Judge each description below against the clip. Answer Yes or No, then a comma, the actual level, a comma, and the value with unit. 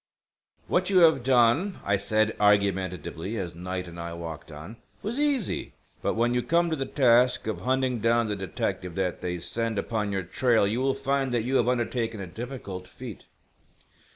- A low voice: Yes, low, 115 Hz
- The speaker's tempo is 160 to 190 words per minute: Yes, average, 180 wpm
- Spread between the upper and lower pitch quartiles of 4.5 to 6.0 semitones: Yes, average, 5.3 semitones